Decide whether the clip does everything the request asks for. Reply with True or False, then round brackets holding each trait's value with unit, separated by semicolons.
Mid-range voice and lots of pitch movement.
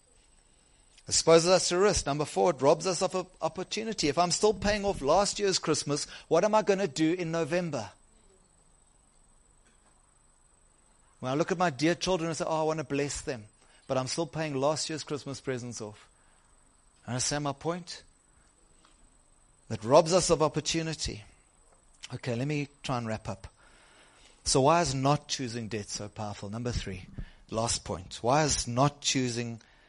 True (145 Hz; 6.3 semitones)